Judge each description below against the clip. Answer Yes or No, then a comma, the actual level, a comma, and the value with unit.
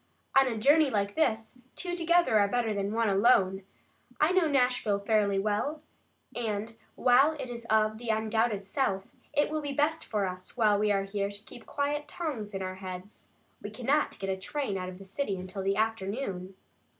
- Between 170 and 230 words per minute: Yes, average, 190 wpm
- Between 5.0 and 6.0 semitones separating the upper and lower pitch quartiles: Yes, average, 5.3 semitones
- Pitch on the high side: Yes, high, 220 Hz